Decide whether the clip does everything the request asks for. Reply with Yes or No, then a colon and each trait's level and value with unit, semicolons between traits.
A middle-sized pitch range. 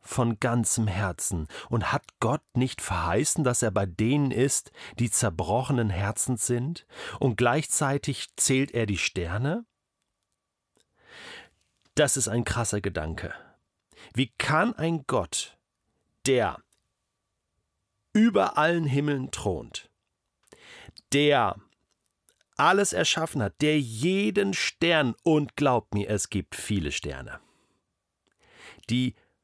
No: wide, 6.0 semitones